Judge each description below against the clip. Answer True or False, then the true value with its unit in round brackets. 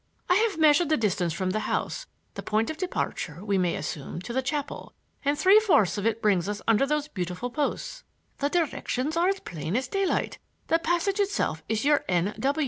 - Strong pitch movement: True (9.0 semitones)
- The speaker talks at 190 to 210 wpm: True (200 wpm)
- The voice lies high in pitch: True (265 Hz)